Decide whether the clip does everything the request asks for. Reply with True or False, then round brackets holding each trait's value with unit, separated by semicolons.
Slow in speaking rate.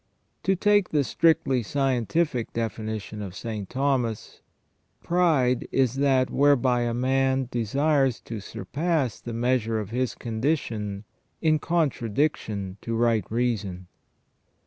True (120 wpm)